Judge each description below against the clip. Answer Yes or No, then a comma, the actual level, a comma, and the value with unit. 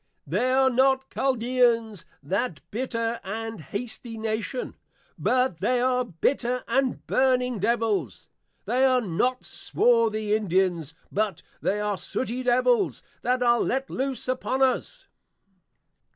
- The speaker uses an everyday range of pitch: Yes, average, 3.1 semitones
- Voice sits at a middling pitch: No, high, 240 Hz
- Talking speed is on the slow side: Yes, slow, 120 wpm